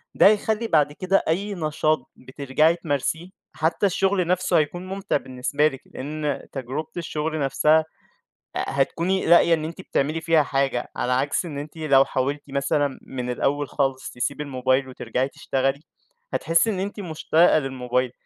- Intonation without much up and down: No, average, 3.7 semitones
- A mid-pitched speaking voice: Yes, medium, 150 Hz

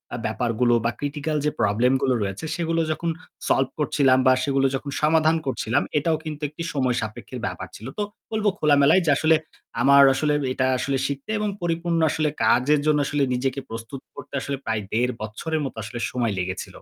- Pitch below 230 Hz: Yes, medium, 140 Hz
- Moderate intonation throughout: Yes, average, 3.8 semitones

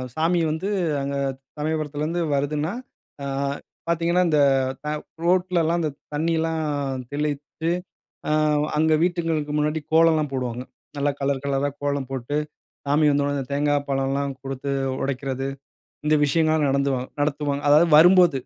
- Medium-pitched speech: Yes, medium, 150 Hz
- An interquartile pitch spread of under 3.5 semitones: Yes, narrow, 2.6 semitones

